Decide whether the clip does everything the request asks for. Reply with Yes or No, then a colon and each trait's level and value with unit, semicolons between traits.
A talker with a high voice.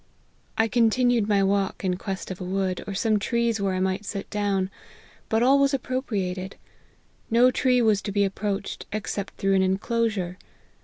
Yes: high, 200 Hz